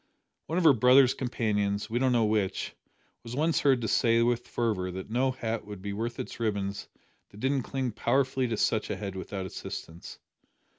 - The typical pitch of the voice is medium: No, low, 115 Hz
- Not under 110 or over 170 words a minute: No, average, 190 wpm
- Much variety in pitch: No, average, 3.9 semitones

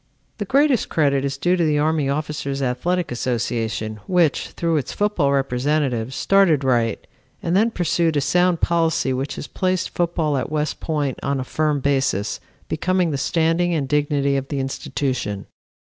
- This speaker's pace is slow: No, average, 165 wpm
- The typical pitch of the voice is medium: Yes, medium, 150 Hz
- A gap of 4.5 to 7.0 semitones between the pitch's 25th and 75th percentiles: No, average, 4.1 semitones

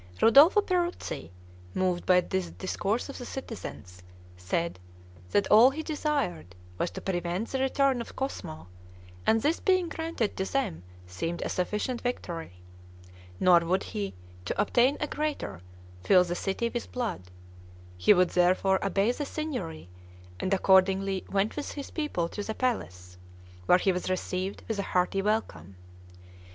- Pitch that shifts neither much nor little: No, wide, 6.7 semitones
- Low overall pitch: No, high, 195 Hz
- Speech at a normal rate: Yes, average, 150 wpm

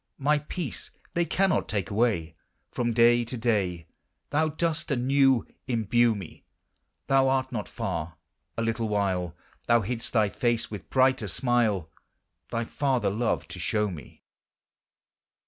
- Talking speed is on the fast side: No, slow, 135 wpm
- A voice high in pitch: No, low, 115 Hz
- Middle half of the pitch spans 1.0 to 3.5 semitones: No, average, 4.4 semitones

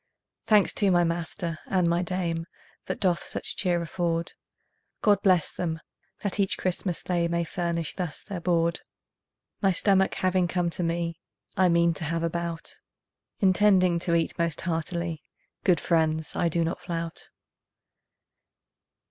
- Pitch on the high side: No, medium, 170 Hz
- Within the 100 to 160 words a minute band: Yes, average, 150 wpm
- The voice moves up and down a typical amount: No, narrow, 1.6 semitones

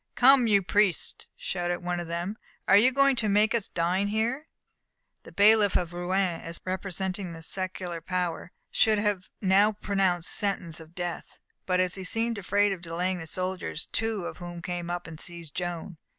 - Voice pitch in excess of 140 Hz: Yes, medium, 185 Hz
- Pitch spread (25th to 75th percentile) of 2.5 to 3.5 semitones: Yes, average, 2.8 semitones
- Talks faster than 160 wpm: Yes, average, 175 wpm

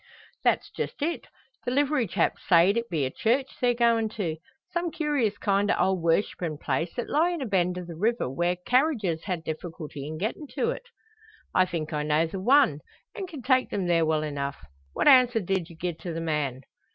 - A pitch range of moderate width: No, wide, 7.4 semitones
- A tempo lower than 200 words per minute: No, fast, 205 wpm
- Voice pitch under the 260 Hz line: Yes, medium, 185 Hz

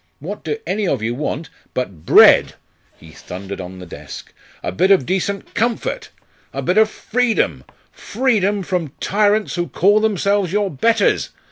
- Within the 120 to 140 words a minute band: No, average, 165 wpm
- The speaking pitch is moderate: No, high, 195 Hz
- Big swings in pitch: Yes, wide, 8.5 semitones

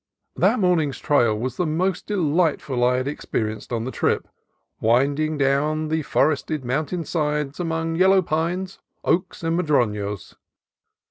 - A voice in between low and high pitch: Yes, medium, 150 Hz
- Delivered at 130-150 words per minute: Yes, average, 140 wpm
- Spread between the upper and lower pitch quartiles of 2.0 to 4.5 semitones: Yes, average, 4.2 semitones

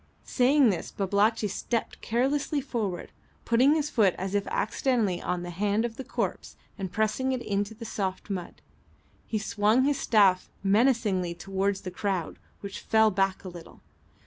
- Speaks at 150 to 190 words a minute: Yes, average, 160 wpm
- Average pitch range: Yes, average, 3.8 semitones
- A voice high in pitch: Yes, high, 210 Hz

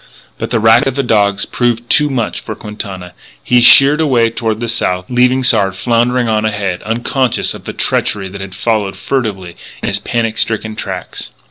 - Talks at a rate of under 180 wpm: No, average, 185 wpm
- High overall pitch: No, low, 115 Hz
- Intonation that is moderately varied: Yes, average, 3.4 semitones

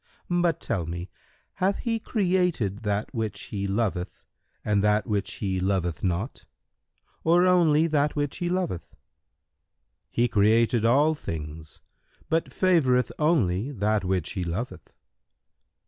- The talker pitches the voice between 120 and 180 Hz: No, low, 110 Hz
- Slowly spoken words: Yes, slow, 120 wpm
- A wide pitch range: Yes, wide, 9.0 semitones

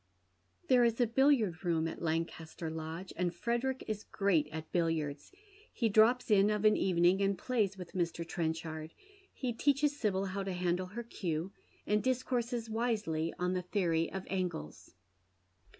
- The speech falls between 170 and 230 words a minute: No, average, 160 wpm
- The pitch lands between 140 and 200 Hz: Yes, high, 190 Hz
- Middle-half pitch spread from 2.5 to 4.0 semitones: No, average, 5.3 semitones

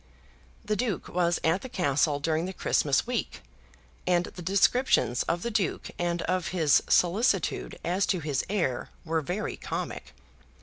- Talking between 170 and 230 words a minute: No, average, 155 wpm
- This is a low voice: No, medium, 175 Hz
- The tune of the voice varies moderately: Yes, average, 3.6 semitones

